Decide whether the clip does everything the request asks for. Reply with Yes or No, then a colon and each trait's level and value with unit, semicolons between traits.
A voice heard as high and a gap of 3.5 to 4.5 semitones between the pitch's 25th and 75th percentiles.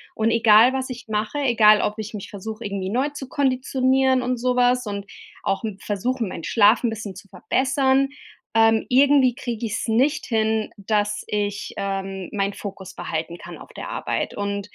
Yes: high, 220 Hz; average, 3.8 semitones